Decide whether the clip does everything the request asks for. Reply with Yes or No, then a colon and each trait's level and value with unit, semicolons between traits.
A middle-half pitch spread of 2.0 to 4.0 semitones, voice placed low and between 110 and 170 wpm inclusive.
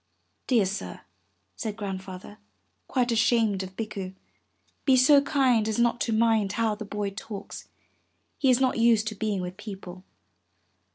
No: average, 3.2 semitones; high, 215 Hz; average, 150 wpm